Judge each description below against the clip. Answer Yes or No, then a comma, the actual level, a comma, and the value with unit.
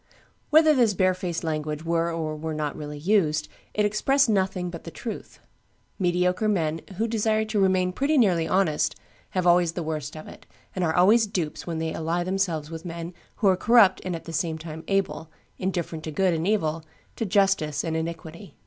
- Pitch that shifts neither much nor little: Yes, average, 3.5 semitones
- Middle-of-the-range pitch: Yes, medium, 175 Hz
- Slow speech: No, average, 190 wpm